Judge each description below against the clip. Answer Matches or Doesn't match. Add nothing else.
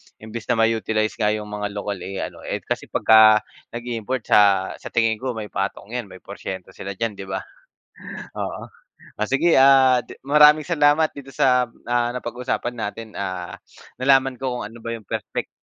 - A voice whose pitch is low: Matches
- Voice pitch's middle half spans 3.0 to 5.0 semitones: Matches